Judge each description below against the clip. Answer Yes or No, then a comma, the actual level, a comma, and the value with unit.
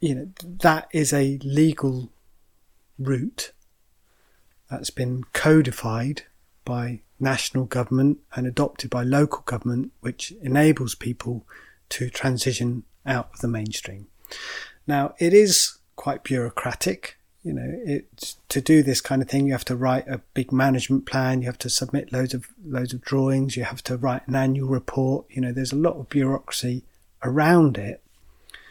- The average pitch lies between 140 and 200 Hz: No, low, 130 Hz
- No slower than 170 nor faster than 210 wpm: No, average, 155 wpm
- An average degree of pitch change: No, narrow, 2.0 semitones